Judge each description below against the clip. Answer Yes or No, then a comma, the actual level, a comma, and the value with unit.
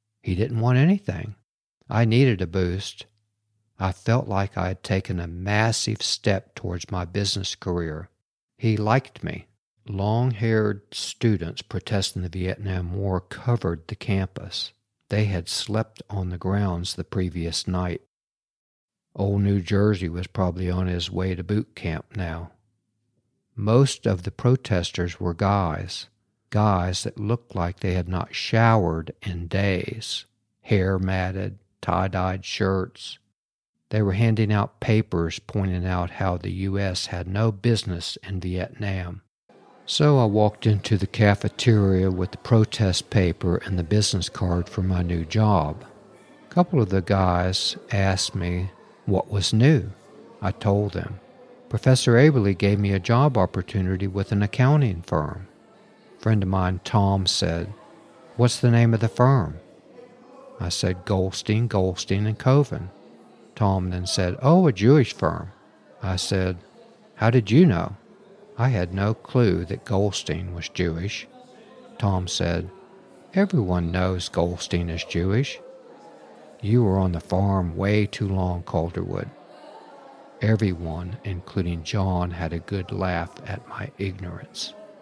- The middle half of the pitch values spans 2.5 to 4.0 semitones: Yes, average, 3.4 semitones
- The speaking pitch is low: Yes, low, 100 Hz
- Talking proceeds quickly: No, average, 140 wpm